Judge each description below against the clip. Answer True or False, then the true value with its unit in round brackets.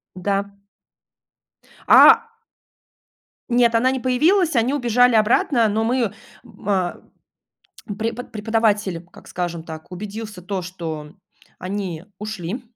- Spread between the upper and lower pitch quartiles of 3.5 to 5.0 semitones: True (4.5 semitones)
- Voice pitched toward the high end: True (210 Hz)